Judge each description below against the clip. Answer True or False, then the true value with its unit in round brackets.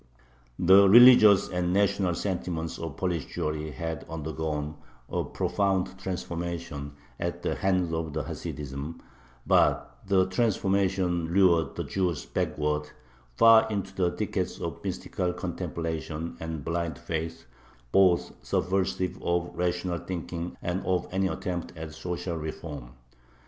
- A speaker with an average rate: False (120 wpm)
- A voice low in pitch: True (85 Hz)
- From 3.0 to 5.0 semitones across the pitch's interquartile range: False (2.6 semitones)